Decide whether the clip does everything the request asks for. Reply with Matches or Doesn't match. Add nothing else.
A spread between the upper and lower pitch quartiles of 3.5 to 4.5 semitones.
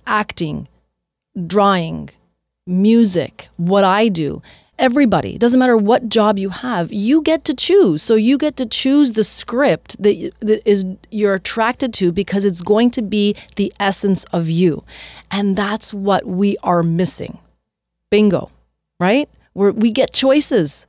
Matches